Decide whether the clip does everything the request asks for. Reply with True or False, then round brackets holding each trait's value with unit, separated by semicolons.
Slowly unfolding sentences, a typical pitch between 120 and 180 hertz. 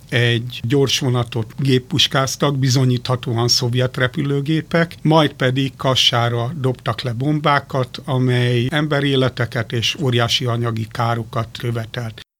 True (100 wpm; 125 Hz)